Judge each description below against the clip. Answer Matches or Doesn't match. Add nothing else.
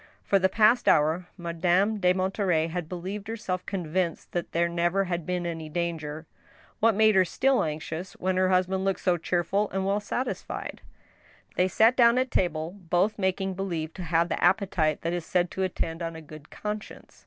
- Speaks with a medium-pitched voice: Matches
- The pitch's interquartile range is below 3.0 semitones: Matches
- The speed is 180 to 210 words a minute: Matches